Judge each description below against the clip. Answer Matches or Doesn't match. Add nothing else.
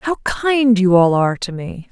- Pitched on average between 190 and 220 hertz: Matches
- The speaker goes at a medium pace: Doesn't match